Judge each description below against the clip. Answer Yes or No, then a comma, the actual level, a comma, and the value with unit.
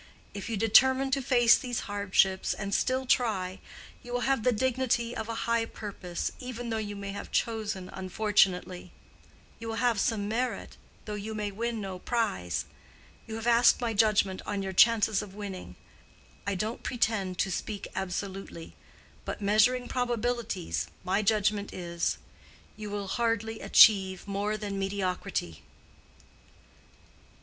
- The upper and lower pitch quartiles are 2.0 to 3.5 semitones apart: Yes, average, 3.1 semitones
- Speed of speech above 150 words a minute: No, average, 140 wpm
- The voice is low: No, high, 210 Hz